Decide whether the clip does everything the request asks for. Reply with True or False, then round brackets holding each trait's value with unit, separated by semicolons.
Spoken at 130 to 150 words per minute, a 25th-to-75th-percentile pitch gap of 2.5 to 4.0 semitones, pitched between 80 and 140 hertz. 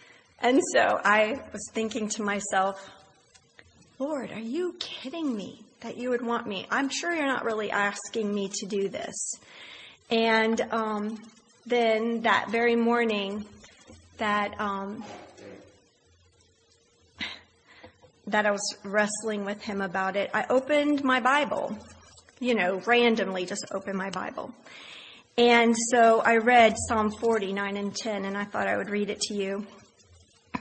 False (140 wpm; 2.9 semitones; 215 Hz)